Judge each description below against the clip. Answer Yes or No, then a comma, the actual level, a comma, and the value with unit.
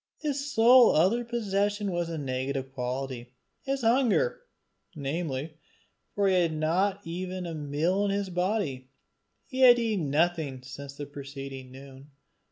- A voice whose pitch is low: No, medium, 170 Hz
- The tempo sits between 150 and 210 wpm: No, average, 140 wpm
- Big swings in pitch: Yes, wide, 6.8 semitones